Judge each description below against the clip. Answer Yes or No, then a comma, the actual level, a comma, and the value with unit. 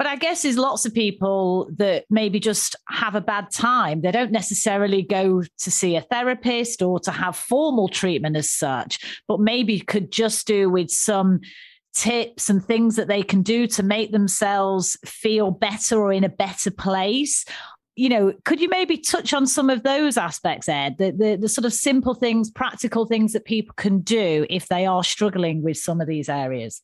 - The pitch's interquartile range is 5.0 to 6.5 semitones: No, average, 3.7 semitones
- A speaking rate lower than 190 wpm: No, average, 195 wpm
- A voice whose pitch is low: No, high, 210 Hz